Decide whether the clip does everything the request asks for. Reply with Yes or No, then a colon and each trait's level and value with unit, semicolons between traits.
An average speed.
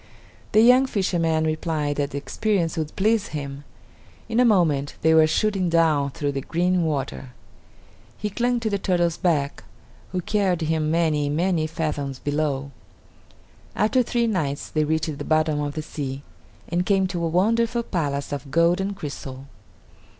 Yes: average, 160 wpm